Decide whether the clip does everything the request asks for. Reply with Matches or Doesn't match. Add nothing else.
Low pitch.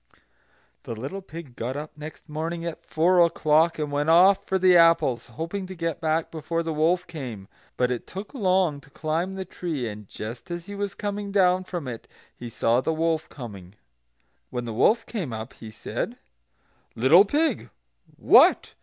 Doesn't match